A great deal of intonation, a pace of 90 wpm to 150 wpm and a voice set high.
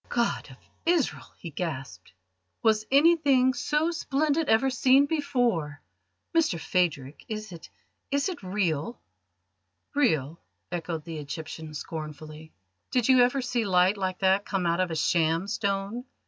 Yes: wide, 8.0 semitones; slow, 135 wpm; high, 195 Hz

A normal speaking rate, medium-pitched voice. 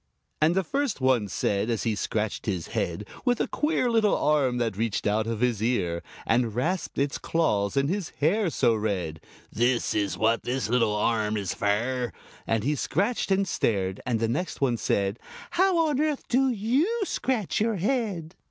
No: average, 180 wpm; low, 125 Hz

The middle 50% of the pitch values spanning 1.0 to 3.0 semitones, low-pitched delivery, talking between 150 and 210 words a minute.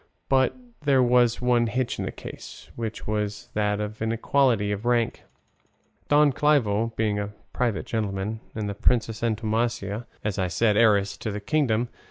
Yes: average, 2.7 semitones; low, 110 Hz; average, 160 wpm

